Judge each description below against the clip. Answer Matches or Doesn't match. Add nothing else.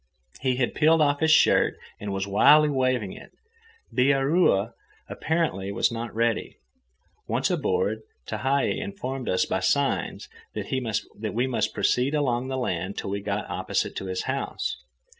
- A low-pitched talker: Matches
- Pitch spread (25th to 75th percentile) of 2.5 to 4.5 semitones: Doesn't match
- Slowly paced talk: Doesn't match